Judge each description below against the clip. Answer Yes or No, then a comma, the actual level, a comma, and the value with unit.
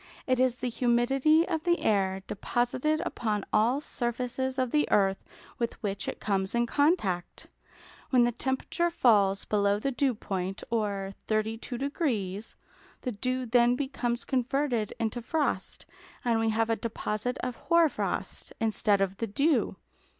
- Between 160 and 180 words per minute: No, average, 145 wpm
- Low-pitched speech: No, high, 240 Hz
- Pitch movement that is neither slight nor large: Yes, average, 3.8 semitones